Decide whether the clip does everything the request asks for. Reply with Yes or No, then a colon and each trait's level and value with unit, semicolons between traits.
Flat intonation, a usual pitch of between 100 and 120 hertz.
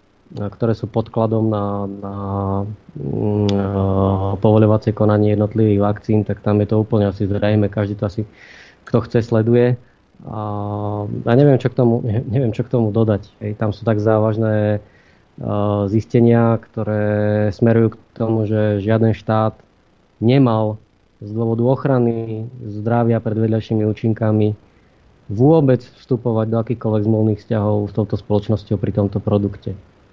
Yes: narrow, 1.6 semitones; low, 110 Hz